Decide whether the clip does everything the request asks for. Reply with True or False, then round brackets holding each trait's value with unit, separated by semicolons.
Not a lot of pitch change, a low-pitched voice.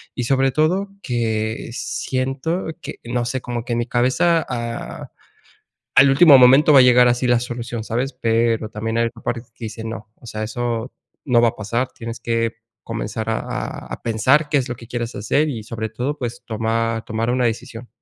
True (2.1 semitones; 120 Hz)